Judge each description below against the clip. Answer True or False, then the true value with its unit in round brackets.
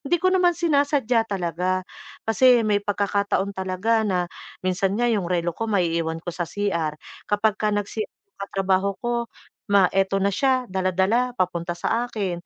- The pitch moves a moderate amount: True (3.8 semitones)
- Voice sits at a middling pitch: False (200 Hz)